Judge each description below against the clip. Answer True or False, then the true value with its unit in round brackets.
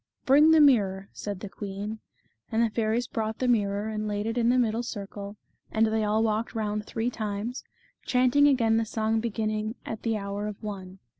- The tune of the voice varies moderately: False (2.0 semitones)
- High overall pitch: True (220 Hz)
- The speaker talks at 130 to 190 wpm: False (205 wpm)